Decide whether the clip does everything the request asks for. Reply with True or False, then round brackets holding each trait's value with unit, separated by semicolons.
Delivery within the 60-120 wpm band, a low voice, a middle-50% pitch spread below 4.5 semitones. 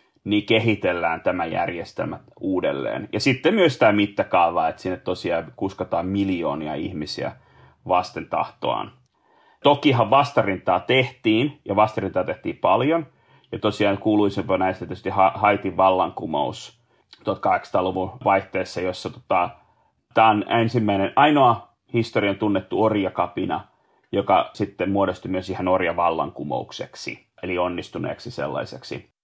True (105 wpm; 105 Hz; 3.8 semitones)